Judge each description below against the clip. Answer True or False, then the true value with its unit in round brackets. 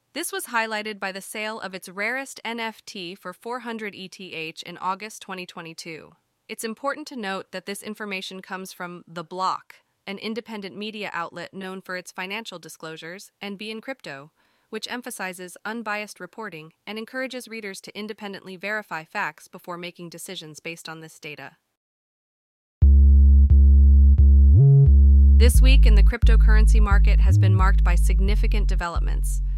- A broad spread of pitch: True (7.5 semitones)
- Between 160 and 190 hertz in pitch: True (185 Hz)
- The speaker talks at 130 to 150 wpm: True (140 wpm)